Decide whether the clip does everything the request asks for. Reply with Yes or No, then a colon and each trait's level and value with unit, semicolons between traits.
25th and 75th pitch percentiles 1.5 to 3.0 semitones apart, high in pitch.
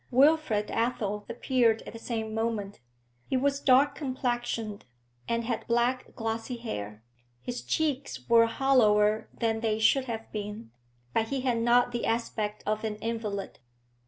Yes: average, 2.7 semitones; high, 230 Hz